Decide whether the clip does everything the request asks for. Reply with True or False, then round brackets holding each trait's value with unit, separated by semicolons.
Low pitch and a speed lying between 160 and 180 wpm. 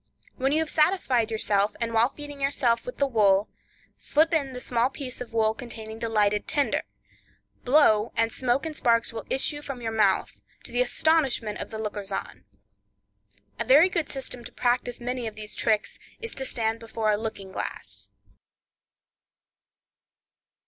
False (240 Hz; 165 wpm)